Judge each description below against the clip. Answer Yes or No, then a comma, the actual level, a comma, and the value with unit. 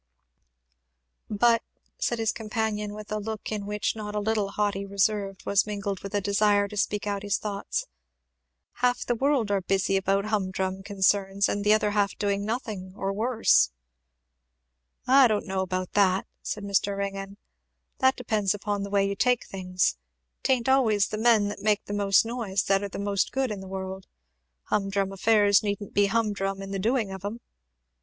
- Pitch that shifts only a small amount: Yes, narrow, 1.6 semitones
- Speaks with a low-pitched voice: No, high, 205 Hz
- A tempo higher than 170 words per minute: Yes, average, 185 wpm